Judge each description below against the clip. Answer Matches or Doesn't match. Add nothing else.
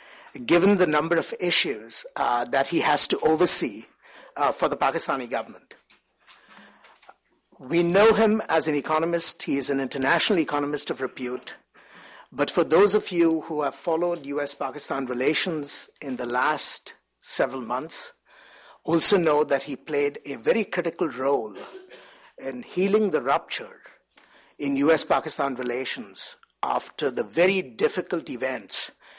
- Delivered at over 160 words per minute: Doesn't match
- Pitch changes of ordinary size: Doesn't match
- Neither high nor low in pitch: Matches